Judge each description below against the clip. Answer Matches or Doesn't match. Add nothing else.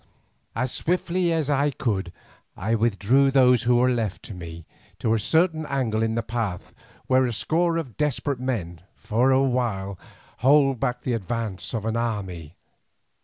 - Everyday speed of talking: Matches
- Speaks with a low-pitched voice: Matches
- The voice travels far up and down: Doesn't match